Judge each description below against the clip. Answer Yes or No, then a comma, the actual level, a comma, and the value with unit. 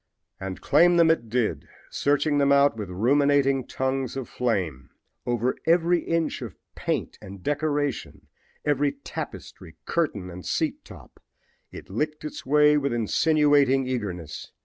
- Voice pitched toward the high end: No, medium, 140 Hz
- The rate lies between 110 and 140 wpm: Yes, slow, 135 wpm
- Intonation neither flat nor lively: Yes, average, 4.5 semitones